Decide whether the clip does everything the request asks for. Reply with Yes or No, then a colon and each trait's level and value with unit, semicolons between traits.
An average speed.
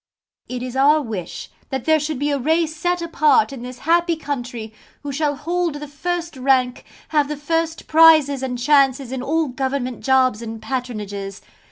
Yes: average, 175 wpm